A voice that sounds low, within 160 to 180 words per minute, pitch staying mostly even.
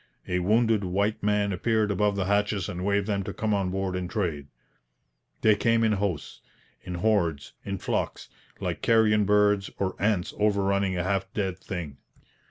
Yes: low, 100 Hz; average, 170 wpm; narrow, 2.2 semitones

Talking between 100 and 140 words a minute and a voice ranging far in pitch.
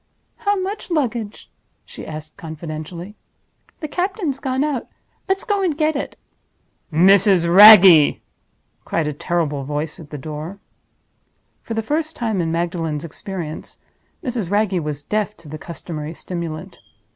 Yes: slow, 135 wpm; wide, 7.7 semitones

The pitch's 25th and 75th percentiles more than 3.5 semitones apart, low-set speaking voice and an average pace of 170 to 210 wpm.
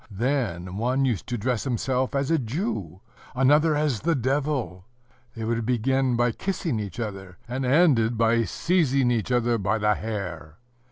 No: average, 4.1 semitones; low, 120 Hz; average, 160 wpm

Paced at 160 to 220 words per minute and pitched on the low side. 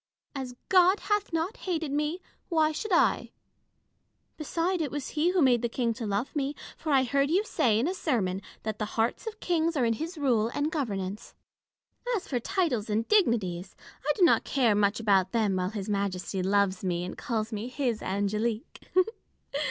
No: average, 190 wpm; high, 245 Hz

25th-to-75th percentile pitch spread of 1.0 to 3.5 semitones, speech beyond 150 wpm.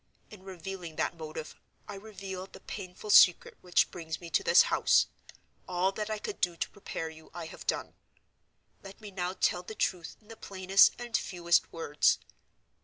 Yes: narrow, 2.5 semitones; average, 180 wpm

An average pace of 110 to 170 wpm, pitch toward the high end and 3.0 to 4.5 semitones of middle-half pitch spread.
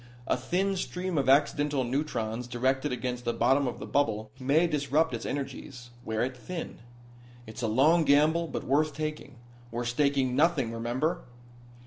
No: average, 155 wpm; low, 135 Hz; average, 3.8 semitones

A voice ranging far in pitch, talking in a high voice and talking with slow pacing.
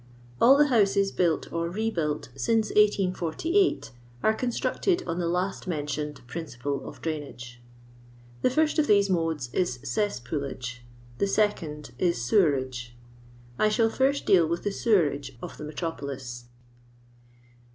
No: wide, 6.9 semitones; medium, 170 Hz; slow, 130 wpm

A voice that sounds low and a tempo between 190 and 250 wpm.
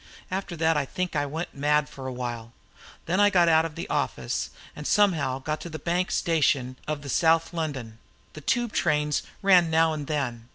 No: medium, 155 Hz; average, 200 wpm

